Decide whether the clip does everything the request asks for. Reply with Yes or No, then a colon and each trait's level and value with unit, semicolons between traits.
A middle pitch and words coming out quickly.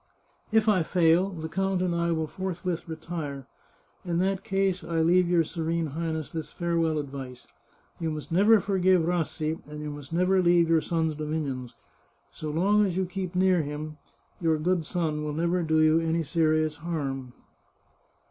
No: medium, 165 Hz; average, 170 wpm